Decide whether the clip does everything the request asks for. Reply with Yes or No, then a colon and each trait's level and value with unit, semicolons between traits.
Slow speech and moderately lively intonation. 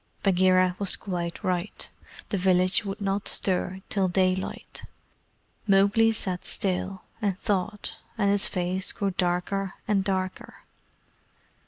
No: slow, 120 wpm; narrow, 1.5 semitones